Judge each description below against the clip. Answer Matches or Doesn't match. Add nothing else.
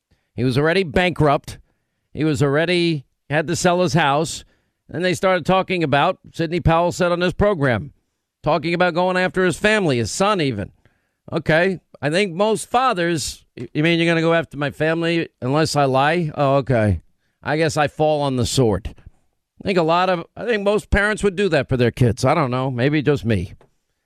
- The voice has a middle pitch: Matches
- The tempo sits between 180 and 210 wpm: Matches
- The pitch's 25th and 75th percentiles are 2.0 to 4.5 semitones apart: Doesn't match